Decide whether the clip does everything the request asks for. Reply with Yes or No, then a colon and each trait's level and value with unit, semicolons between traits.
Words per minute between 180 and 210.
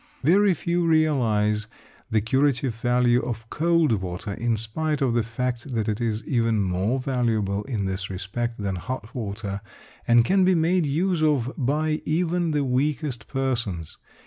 No: average, 155 wpm